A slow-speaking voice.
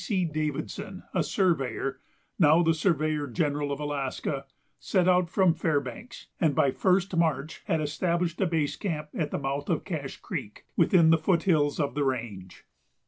No: average, 165 wpm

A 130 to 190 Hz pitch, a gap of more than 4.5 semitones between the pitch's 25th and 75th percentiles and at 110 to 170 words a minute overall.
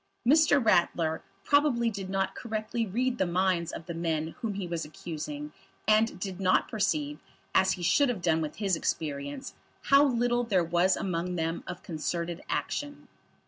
Yes: medium, 185 Hz; average, 5.3 semitones; average, 165 wpm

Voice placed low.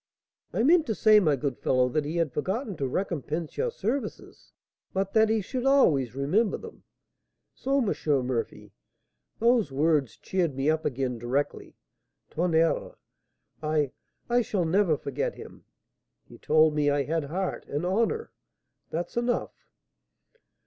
No: medium, 165 Hz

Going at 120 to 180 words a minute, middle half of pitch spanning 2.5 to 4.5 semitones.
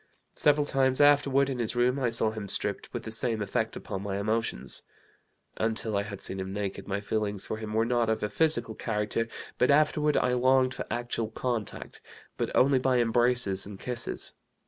No: average, 190 wpm; average, 3.4 semitones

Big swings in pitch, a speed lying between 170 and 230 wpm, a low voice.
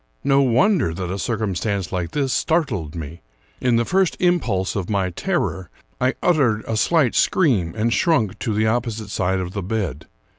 Yes: wide, 5.9 semitones; average, 175 wpm; low, 110 Hz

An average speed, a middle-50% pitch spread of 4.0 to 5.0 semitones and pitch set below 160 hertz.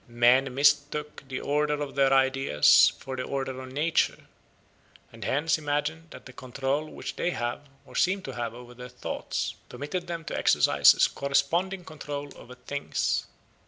No: average, 160 wpm; narrow, 2.6 semitones; medium, 140 Hz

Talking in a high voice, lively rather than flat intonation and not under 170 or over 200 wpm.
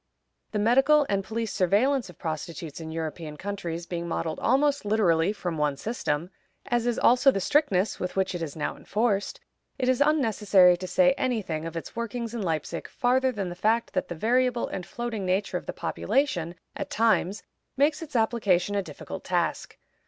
Yes: high, 205 Hz; wide, 5.7 semitones; average, 180 wpm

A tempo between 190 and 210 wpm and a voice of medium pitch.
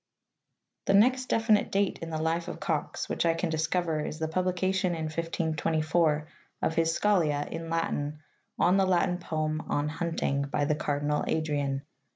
No: average, 165 wpm; medium, 165 Hz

